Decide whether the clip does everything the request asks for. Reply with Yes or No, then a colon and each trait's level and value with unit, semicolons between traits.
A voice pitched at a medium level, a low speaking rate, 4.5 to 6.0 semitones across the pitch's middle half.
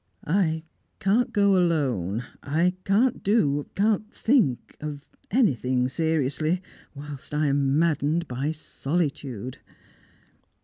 Yes: medium, 155 Hz; slow, 100 wpm; average, 5.3 semitones